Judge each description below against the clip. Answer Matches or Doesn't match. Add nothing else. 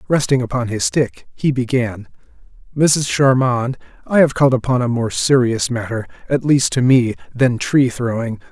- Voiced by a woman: Doesn't match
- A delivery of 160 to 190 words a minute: Doesn't match